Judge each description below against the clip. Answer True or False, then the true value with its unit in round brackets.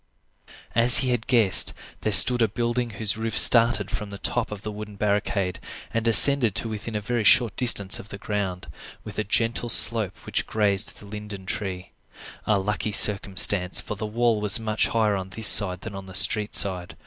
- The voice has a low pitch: True (105 Hz)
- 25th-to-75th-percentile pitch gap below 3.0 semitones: True (2.5 semitones)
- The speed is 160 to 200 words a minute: True (195 wpm)